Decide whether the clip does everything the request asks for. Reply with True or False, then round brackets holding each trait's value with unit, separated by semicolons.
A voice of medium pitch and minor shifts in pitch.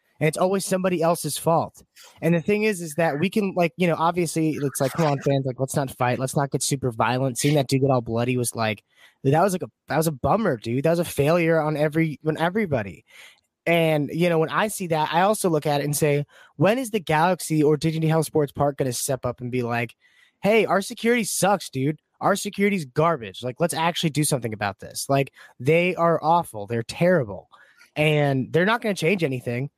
False (155 Hz; 4.2 semitones)